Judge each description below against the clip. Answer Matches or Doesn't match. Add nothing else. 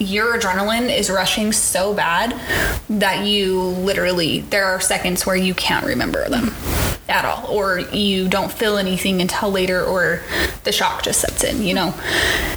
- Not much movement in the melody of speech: Matches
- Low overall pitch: Doesn't match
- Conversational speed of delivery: Matches